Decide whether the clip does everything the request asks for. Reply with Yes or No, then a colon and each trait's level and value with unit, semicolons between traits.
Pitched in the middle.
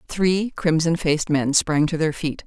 Yes: medium, 160 Hz